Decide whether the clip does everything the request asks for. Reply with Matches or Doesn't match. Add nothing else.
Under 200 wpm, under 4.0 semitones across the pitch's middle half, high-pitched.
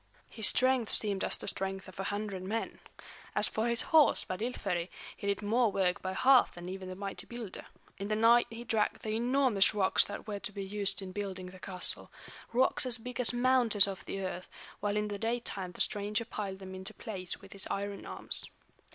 Doesn't match